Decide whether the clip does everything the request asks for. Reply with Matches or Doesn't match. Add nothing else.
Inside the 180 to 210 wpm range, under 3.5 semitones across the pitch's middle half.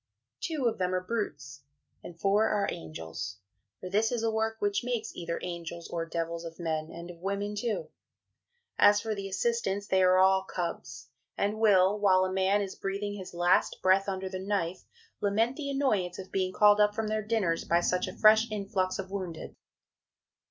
Matches